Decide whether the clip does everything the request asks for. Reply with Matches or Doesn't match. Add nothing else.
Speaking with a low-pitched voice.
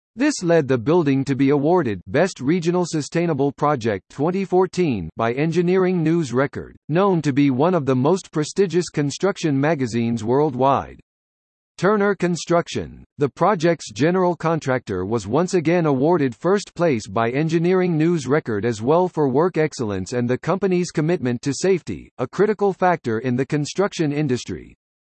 Doesn't match